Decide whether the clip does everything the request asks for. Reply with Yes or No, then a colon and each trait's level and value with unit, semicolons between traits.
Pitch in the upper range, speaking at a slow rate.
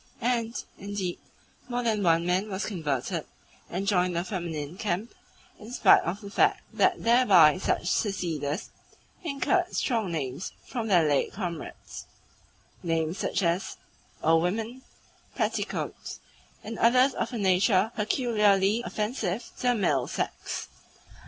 Yes: high, 200 Hz; slow, 130 wpm